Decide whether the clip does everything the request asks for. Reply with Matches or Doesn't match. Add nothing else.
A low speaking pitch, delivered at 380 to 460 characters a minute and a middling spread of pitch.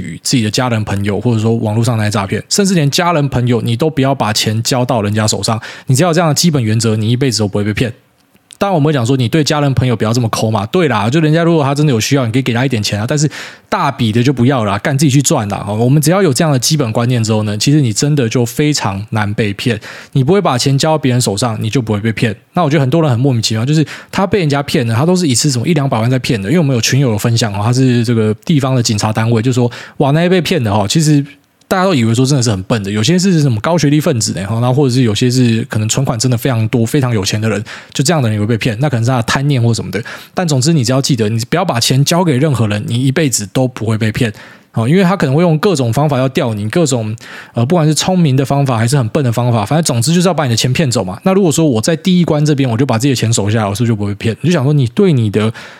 Matches